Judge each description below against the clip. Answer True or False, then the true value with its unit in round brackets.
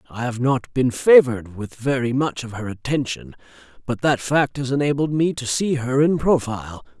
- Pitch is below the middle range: True (130 Hz)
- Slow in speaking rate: False (190 wpm)